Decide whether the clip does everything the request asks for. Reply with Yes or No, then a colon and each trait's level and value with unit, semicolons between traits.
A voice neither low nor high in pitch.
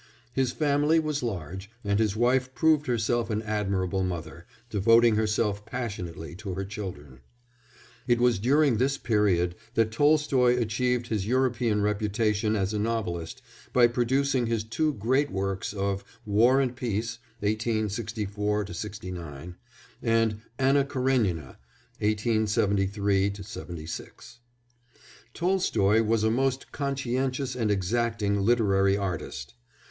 No: low, 110 Hz